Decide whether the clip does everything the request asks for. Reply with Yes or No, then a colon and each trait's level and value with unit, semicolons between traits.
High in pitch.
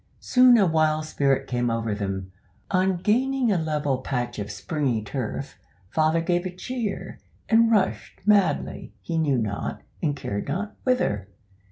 No: medium, 155 Hz